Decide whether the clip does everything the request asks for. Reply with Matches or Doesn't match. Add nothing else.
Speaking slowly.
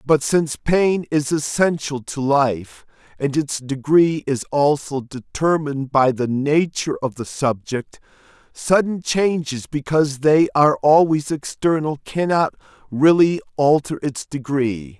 Matches